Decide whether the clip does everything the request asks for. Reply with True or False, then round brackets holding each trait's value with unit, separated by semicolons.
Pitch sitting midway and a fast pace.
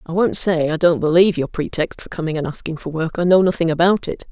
True (165 Hz; 265 wpm)